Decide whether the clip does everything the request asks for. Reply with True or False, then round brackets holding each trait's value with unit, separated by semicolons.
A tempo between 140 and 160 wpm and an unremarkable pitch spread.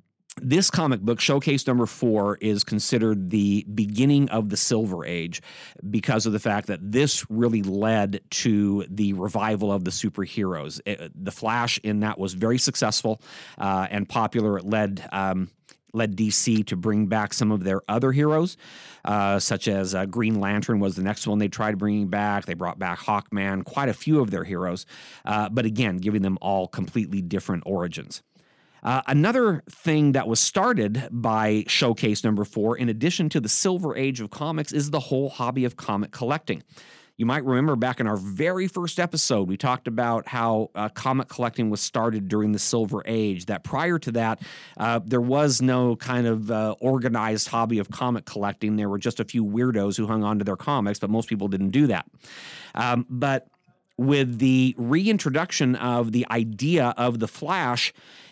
False (185 wpm; 3.8 semitones)